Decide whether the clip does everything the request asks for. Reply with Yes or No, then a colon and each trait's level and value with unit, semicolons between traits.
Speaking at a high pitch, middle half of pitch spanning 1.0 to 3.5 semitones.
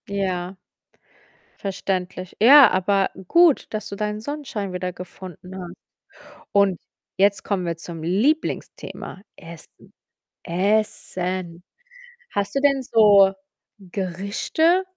Yes: high, 195 Hz; average, 2.8 semitones